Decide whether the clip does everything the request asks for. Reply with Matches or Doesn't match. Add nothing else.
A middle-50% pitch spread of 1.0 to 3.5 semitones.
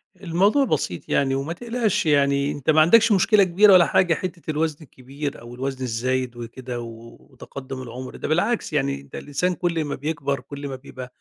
Doesn't match